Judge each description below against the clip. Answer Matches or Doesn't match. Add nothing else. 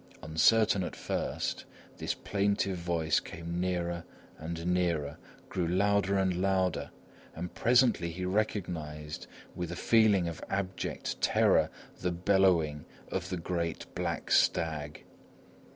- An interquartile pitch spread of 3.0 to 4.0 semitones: Doesn't match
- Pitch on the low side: Matches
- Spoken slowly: Matches